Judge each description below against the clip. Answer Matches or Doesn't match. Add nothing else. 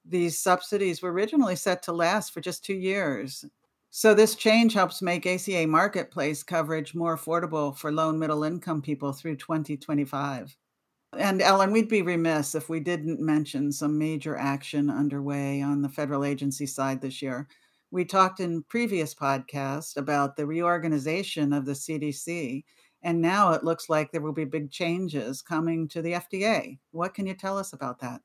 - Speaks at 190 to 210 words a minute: Doesn't match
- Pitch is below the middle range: Doesn't match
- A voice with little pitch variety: Doesn't match